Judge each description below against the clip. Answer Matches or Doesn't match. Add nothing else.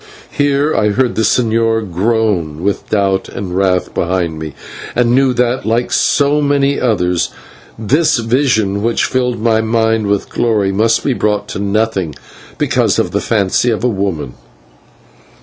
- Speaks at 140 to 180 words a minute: Matches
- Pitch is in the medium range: Doesn't match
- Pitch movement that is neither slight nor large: Matches